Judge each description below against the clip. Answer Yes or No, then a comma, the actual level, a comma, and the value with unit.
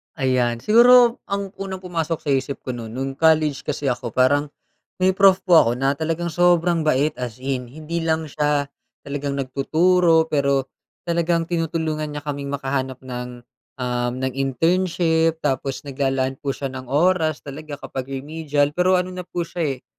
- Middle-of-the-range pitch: Yes, medium, 150 Hz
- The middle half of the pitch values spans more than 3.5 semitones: Yes, average, 3.9 semitones